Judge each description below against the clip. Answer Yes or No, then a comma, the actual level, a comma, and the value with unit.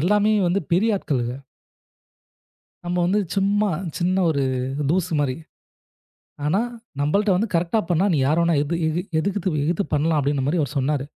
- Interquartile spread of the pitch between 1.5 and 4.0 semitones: No, average, 4.5 semitones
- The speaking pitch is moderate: Yes, medium, 170 Hz